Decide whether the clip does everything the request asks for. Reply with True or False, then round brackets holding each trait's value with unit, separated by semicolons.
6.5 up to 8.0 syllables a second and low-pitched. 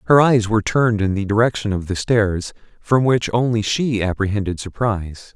False (5.3 syllables/s; 105 Hz)